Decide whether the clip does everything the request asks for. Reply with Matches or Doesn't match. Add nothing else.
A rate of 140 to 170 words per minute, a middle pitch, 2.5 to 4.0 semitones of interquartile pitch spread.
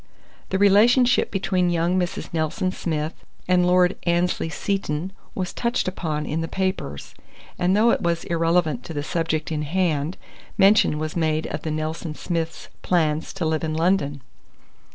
Matches